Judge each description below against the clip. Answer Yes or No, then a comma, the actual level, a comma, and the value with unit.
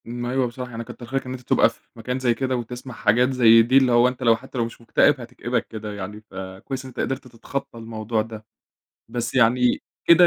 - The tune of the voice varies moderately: No, narrow, 2.1 semitones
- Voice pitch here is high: No, low, 120 Hz